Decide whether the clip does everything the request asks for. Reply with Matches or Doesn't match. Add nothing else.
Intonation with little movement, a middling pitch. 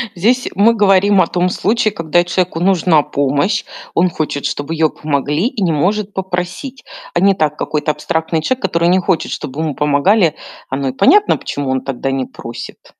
Doesn't match